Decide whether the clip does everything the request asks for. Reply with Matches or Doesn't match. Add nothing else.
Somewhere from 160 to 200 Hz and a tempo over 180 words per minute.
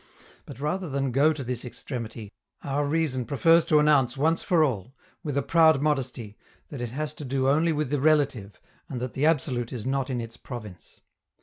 Doesn't match